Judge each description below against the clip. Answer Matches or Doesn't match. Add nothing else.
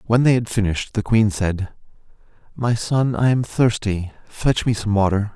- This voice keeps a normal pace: Matches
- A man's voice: Matches